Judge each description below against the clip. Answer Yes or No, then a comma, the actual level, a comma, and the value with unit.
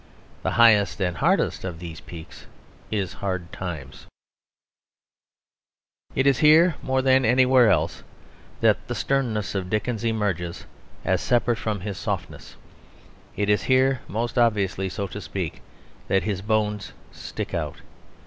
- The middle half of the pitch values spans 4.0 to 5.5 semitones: Yes, average, 4.5 semitones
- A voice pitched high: No, low, 105 Hz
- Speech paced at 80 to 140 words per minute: Yes, slow, 135 wpm